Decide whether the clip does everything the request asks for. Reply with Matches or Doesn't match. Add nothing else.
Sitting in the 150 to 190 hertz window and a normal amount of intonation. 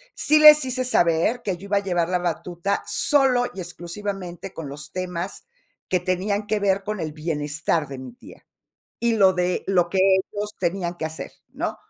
Matches